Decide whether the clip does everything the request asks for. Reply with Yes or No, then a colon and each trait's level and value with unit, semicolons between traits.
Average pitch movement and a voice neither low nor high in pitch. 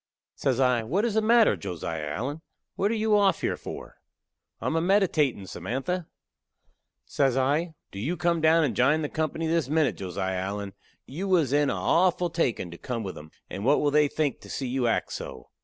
No: wide, 6.5 semitones; medium, 145 Hz